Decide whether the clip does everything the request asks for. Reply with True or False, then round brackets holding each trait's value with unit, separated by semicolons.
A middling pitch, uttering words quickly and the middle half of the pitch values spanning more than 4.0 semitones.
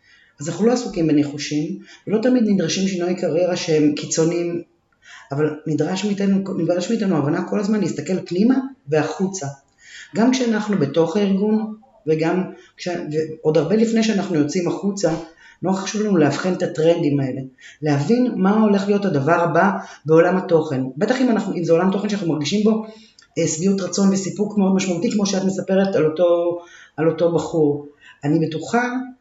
True (175 Hz; 155 wpm; 4.4 semitones)